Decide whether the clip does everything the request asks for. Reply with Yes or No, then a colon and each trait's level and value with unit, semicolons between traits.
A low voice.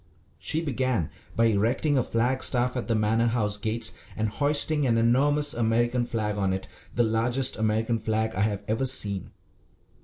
Yes: low, 115 Hz